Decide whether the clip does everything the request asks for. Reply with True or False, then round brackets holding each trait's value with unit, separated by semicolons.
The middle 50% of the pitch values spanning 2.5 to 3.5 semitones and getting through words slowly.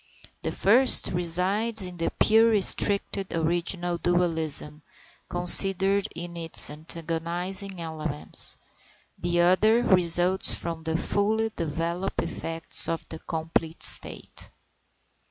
True (2.9 semitones; 100 wpm)